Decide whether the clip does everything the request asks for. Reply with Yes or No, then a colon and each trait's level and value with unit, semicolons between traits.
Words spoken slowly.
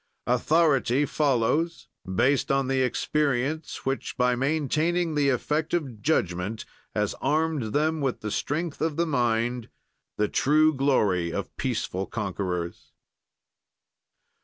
Yes: slow, 115 wpm